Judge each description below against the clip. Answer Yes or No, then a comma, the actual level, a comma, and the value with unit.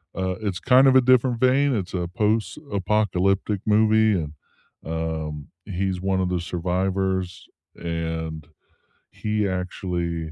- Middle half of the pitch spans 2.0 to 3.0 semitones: No, average, 3.8 semitones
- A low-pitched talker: Yes, very low, 95 Hz